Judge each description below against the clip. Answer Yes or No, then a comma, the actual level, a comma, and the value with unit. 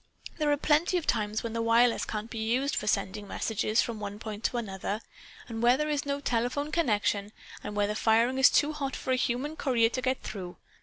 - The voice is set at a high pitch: Yes, high, 230 Hz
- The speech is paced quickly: Yes, fast, 220 wpm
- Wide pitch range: No, average, 4.2 semitones